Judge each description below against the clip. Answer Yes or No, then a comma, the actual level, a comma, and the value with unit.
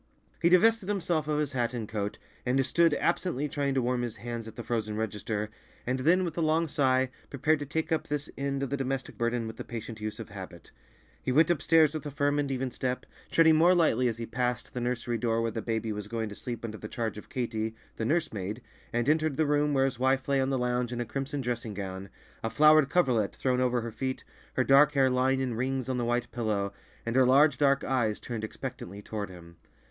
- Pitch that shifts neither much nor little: Yes, average, 4.0 semitones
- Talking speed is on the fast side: Yes, fast, 235 wpm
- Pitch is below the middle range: Yes, low, 125 Hz